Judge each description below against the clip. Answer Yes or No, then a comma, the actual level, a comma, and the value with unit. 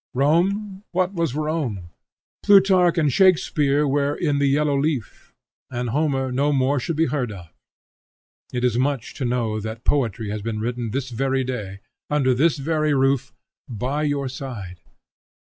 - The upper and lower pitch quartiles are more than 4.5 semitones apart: No, average, 3.8 semitones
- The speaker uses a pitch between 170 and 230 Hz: No, low, 135 Hz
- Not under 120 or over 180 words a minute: Yes, average, 155 wpm